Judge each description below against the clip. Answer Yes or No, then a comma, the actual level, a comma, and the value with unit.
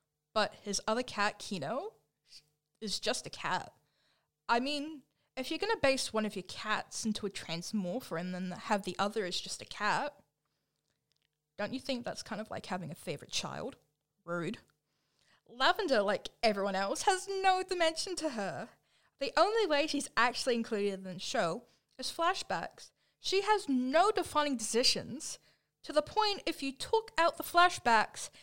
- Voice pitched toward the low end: No, high, 240 Hz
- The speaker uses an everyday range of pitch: No, wide, 8.7 semitones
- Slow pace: No, average, 165 wpm